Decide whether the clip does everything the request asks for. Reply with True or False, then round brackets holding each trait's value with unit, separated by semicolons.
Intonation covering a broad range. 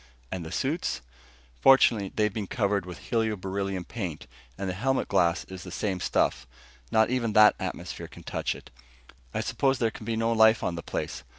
False (3.6 semitones)